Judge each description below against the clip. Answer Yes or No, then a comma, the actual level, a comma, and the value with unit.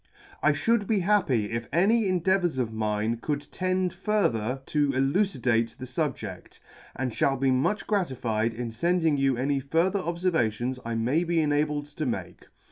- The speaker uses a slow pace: No, average, 160 wpm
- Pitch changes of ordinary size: No, wide, 6.9 semitones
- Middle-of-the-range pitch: Yes, medium, 145 Hz